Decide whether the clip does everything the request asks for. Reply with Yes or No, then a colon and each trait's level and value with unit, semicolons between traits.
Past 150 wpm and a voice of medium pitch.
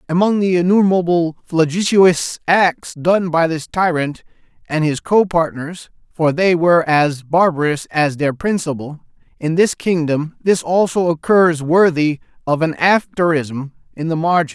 No: average, 140 wpm; medium, 165 Hz